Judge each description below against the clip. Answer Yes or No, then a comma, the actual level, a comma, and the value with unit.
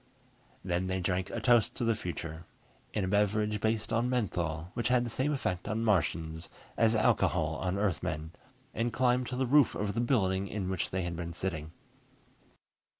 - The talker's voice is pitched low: Yes, low, 100 Hz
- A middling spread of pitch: Yes, average, 4.6 semitones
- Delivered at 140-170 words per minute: No, average, 180 wpm